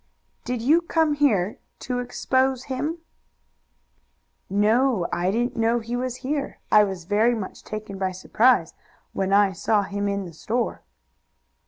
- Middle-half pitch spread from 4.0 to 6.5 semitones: Yes, average, 4.3 semitones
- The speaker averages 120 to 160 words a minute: Yes, average, 145 wpm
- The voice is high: Yes, high, 225 Hz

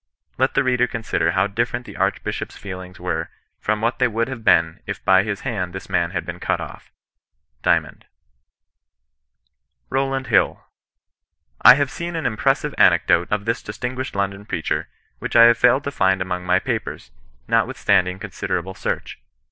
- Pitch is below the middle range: Yes, low, 105 Hz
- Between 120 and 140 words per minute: No, average, 165 wpm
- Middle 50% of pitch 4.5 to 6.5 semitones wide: Yes, average, 5.1 semitones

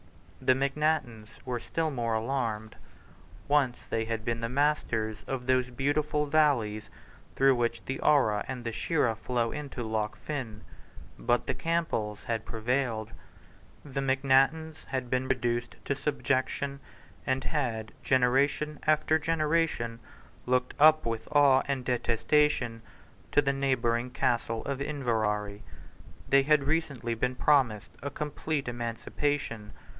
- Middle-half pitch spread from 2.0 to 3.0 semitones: No, average, 3.8 semitones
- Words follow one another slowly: Yes, slow, 130 wpm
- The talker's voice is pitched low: Yes, low, 130 Hz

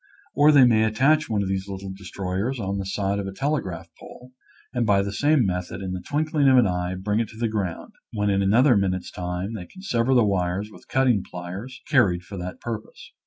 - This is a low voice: Yes, low, 100 Hz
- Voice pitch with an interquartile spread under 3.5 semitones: No, average, 4.6 semitones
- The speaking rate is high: Yes, fast, 220 wpm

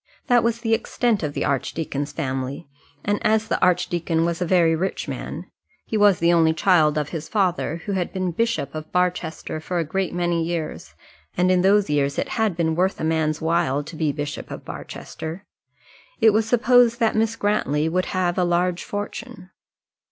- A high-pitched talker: No, medium, 175 Hz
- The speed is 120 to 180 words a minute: No, average, 190 wpm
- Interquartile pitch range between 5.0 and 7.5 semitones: No, average, 4.3 semitones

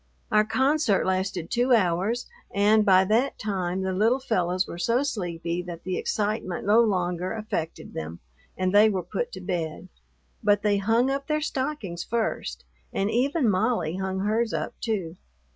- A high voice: Yes, high, 200 Hz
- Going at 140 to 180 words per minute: Yes, average, 160 wpm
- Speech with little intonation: No, average, 4.0 semitones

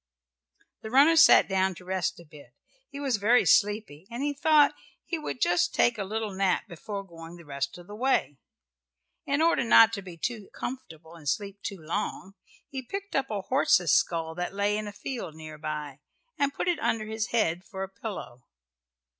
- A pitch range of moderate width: No, wide, 5.8 semitones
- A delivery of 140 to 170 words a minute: No, average, 195 wpm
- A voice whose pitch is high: Yes, high, 200 Hz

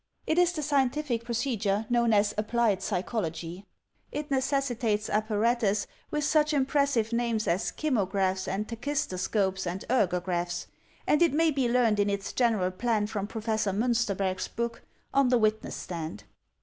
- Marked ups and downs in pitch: No, average, 4.6 semitones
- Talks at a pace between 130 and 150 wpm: Yes, average, 140 wpm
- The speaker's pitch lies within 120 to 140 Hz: No, high, 225 Hz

